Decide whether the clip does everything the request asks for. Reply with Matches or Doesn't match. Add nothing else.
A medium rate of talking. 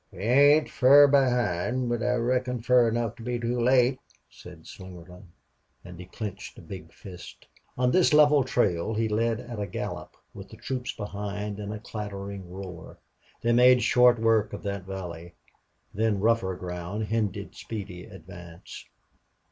Matches